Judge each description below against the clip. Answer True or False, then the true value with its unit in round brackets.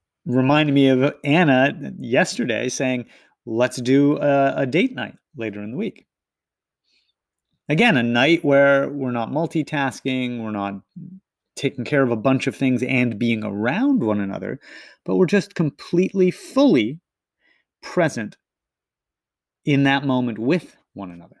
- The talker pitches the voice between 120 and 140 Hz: True (135 Hz)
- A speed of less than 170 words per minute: True (135 wpm)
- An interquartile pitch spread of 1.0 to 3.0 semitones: False (3.4 semitones)